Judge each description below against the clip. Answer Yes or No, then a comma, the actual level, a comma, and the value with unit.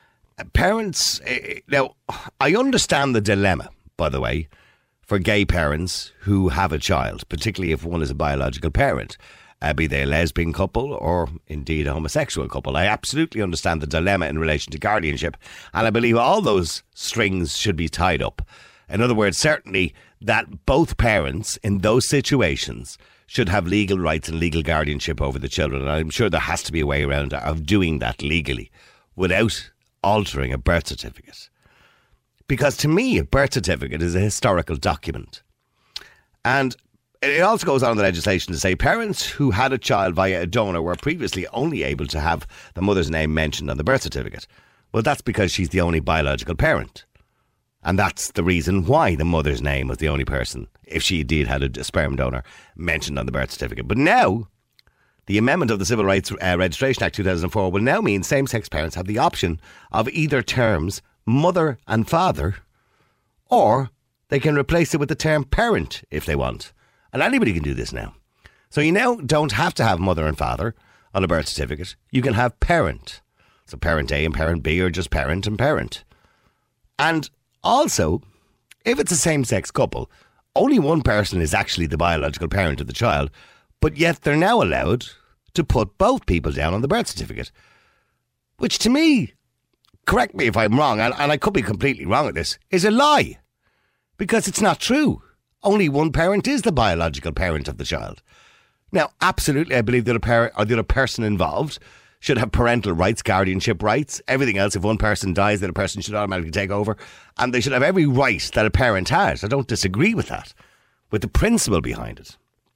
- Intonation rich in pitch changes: Yes, wide, 7.5 semitones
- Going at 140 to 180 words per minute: No, average, 190 wpm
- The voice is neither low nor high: No, very low, 95 Hz